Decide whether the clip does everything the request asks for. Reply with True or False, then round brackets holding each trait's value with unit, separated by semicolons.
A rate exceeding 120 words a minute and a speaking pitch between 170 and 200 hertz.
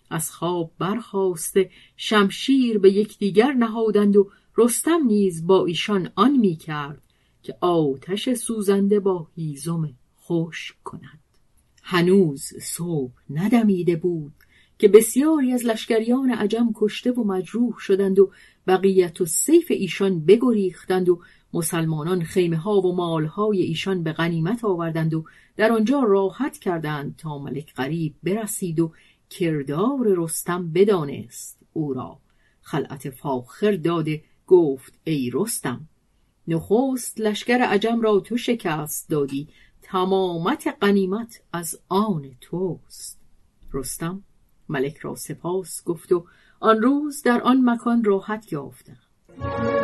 False (115 wpm; 185 Hz)